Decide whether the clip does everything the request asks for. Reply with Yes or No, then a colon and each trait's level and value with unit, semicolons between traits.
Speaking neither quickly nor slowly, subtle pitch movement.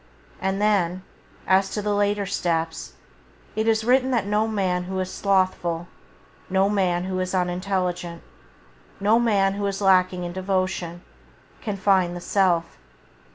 Yes: average, 145 wpm; narrow, 2.2 semitones